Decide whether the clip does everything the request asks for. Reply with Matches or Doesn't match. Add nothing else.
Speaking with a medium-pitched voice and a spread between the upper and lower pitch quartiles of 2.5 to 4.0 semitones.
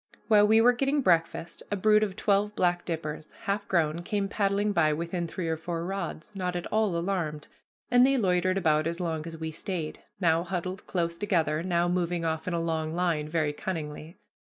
Matches